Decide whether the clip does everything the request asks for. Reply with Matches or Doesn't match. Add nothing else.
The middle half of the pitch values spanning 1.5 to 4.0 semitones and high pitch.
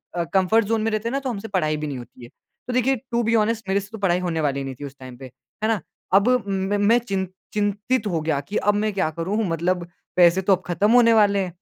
Doesn't match